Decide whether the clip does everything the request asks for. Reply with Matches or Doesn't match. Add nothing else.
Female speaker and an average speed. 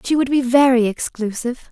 Matches